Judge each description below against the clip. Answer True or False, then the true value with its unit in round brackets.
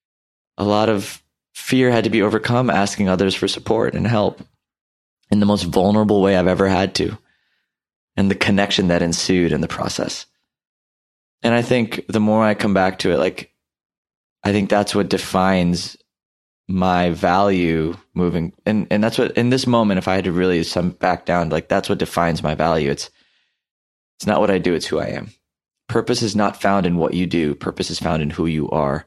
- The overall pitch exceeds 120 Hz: False (95 Hz)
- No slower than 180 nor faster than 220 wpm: True (200 wpm)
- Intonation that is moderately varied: True (3.3 semitones)